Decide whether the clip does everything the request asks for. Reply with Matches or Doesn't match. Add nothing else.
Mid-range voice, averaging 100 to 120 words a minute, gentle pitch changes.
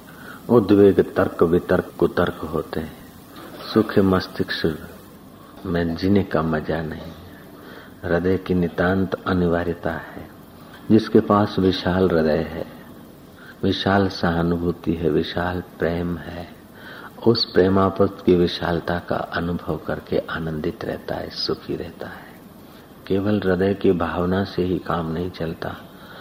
Doesn't match